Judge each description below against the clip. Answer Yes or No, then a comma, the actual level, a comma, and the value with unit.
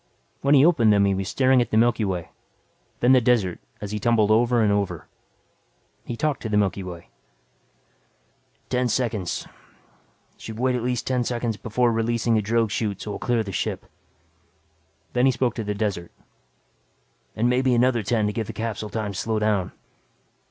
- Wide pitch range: No, average, 2.8 semitones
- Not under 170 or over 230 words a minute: Yes, average, 180 wpm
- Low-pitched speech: Yes, low, 115 Hz